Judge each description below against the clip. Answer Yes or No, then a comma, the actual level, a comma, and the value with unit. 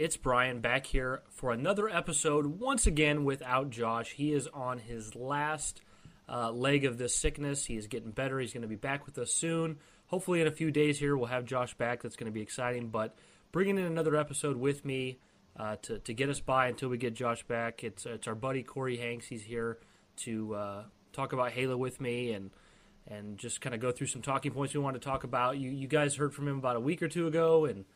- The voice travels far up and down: No, average, 3.5 semitones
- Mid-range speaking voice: No, low, 130 Hz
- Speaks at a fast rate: Yes, fast, 235 wpm